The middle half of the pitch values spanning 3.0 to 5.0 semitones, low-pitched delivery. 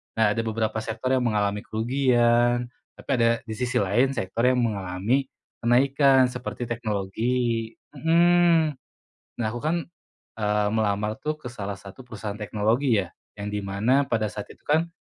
Yes: average, 3.3 semitones; low, 115 Hz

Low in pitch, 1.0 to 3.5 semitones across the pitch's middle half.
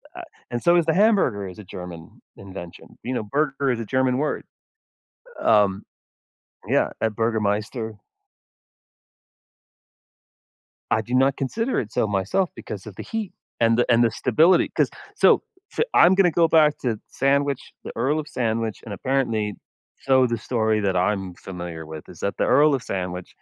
No: low, 115 Hz; wide, 5.4 semitones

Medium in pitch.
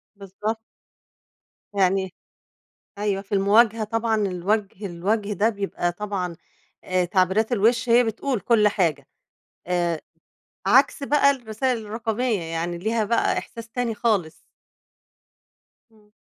No: high, 210 Hz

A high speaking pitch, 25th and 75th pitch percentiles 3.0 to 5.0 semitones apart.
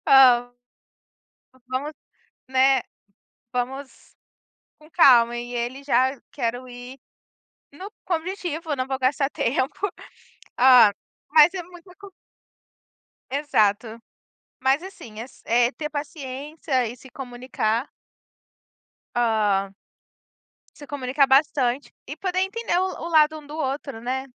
Yes: very high, 265 Hz; average, 3.7 semitones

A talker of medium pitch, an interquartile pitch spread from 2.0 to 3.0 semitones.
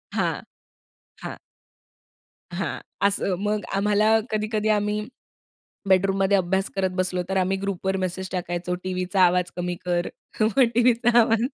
No: high, 195 Hz; narrow, 2.5 semitones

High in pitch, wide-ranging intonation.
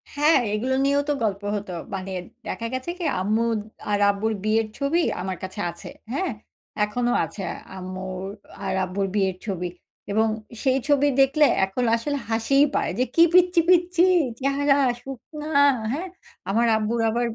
Yes: high, 230 Hz; wide, 6.3 semitones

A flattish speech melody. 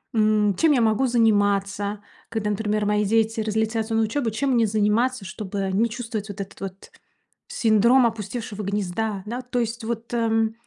Yes: narrow, 2.0 semitones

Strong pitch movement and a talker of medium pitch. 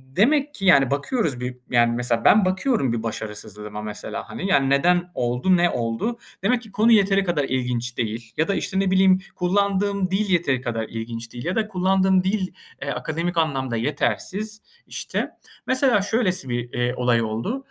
Yes: wide, 8.3 semitones; medium, 170 Hz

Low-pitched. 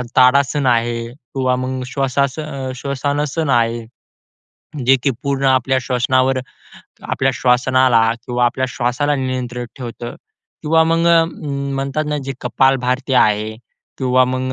Yes: low, 130 Hz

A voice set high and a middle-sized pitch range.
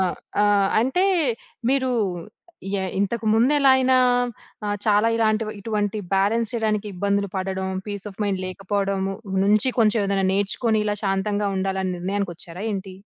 No: high, 205 Hz; narrow, 2.3 semitones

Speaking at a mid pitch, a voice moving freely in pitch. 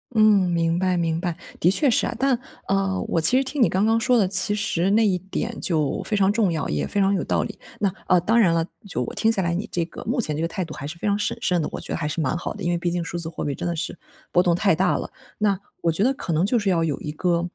No: medium, 180 Hz; average, 3.7 semitones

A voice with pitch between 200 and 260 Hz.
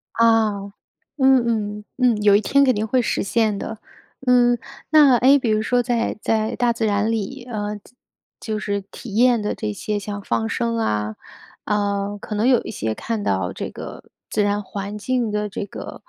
Yes: high, 215 Hz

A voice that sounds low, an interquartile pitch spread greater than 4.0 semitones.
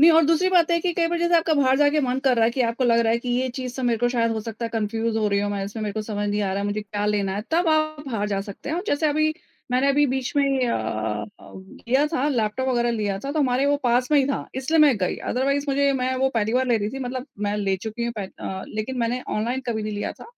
No: high, 245 Hz; average, 4.7 semitones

